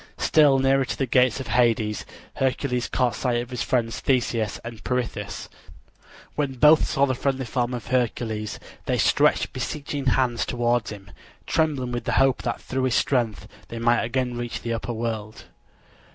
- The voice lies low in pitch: Yes, low, 125 Hz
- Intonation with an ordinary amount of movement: No, narrow, 2.3 semitones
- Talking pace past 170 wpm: No, average, 165 wpm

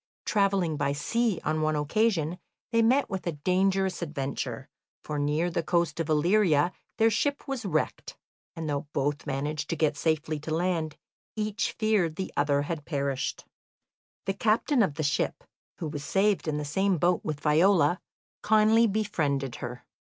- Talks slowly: No, average, 160 wpm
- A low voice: No, medium, 165 Hz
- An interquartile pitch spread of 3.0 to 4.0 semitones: No, average, 5.1 semitones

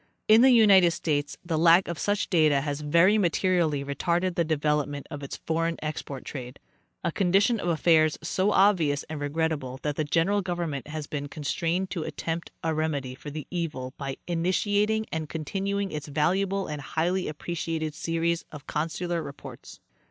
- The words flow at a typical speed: Yes, average, 165 wpm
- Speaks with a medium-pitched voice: Yes, medium, 160 Hz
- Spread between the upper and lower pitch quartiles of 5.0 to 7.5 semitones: No, average, 3.3 semitones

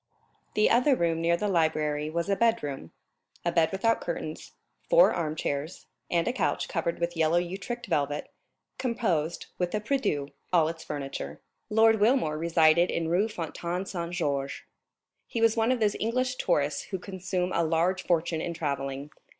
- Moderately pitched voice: Yes, medium, 170 Hz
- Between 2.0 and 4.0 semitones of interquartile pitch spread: No, average, 4.9 semitones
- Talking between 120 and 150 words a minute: No, average, 165 wpm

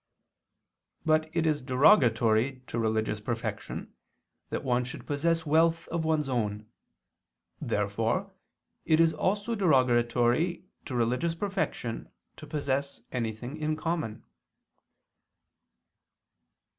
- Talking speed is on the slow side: Yes, slow, 100 wpm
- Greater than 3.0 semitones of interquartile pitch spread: Yes, wide, 5.6 semitones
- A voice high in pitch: No, low, 135 Hz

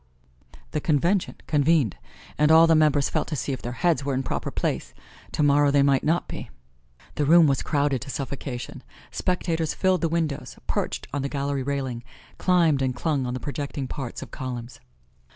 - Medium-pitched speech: Yes, medium, 145 Hz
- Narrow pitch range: No, average, 3.0 semitones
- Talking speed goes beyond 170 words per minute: Yes, average, 180 wpm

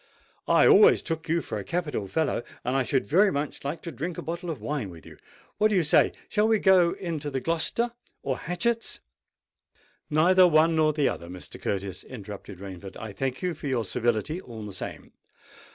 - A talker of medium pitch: Yes, medium, 150 Hz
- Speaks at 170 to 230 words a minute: Yes, average, 195 wpm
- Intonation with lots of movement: Yes, wide, 7.1 semitones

